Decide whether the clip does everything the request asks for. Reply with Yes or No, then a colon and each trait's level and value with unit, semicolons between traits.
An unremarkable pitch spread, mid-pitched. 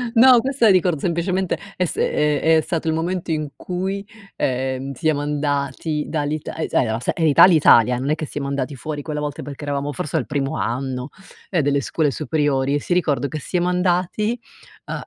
Yes: average, 3.9 semitones; medium, 150 Hz